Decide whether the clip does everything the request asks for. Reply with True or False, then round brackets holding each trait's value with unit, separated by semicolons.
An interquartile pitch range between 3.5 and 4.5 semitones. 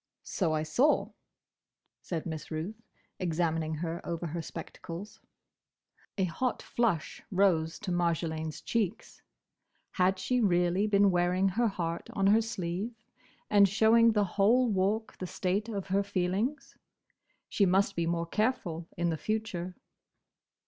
True (3.8 semitones)